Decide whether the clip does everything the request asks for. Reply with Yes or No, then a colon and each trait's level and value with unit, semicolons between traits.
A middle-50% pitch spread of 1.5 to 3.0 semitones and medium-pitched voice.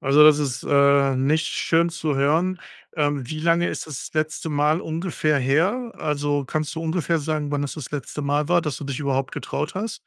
Yes: narrow, 2.4 semitones; medium, 150 Hz